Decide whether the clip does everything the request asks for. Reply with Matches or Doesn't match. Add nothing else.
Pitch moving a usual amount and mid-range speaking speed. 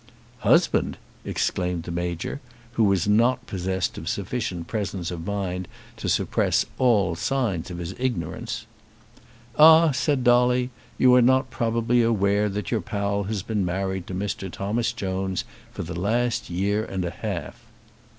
Matches